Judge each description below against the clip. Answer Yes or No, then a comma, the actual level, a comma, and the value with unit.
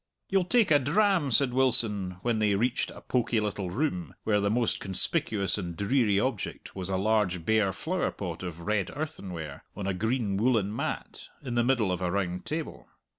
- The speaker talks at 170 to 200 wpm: Yes, average, 180 wpm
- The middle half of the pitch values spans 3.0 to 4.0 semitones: No, average, 5.3 semitones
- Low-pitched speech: Yes, low, 105 Hz